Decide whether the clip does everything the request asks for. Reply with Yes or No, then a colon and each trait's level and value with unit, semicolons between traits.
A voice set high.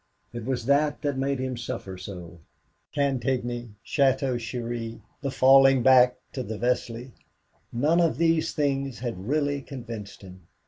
No: low, 125 Hz